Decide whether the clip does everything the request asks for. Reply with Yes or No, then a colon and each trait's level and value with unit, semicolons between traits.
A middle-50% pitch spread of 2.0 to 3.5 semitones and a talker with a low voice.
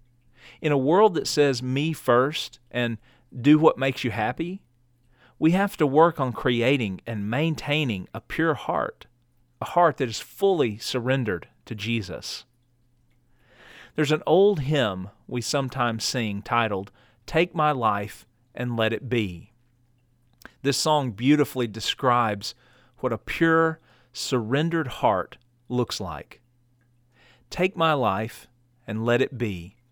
Yes: average, 3.2 semitones; low, 125 Hz